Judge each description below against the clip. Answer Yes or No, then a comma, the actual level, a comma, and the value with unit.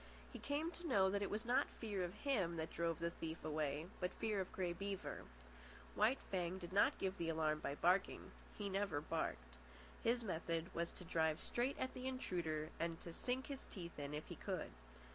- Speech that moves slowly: No, average, 200 wpm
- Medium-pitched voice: Yes, medium, 180 Hz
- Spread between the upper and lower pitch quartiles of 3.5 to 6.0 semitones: Yes, average, 4.6 semitones